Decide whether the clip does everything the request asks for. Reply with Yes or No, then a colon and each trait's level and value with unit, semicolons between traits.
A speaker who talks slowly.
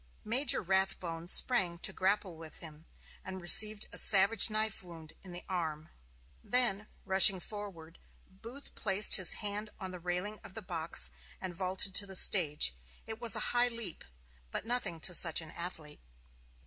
No: average, 160 wpm